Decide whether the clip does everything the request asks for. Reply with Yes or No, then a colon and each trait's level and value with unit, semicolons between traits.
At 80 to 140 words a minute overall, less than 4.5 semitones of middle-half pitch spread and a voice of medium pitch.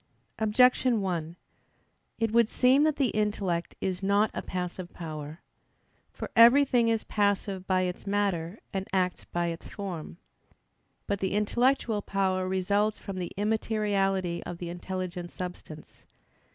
No: slow, 135 wpm; average, 3.1 semitones; high, 195 Hz